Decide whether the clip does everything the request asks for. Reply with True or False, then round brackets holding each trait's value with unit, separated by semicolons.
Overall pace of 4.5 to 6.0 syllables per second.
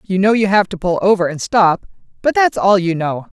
True (5.3 syllables/s)